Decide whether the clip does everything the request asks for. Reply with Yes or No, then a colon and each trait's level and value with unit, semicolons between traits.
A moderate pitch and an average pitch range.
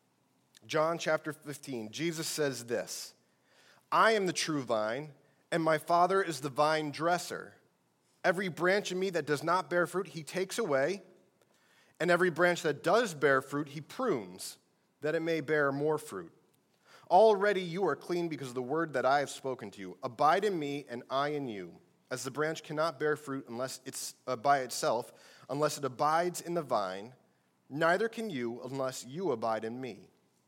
Yes: medium, 150 Hz; average, 4.3 semitones